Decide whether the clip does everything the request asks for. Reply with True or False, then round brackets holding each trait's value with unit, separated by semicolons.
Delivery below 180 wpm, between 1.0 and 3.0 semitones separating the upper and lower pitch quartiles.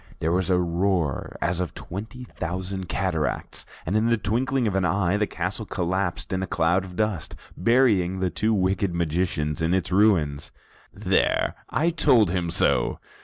False (170 wpm; 3.4 semitones)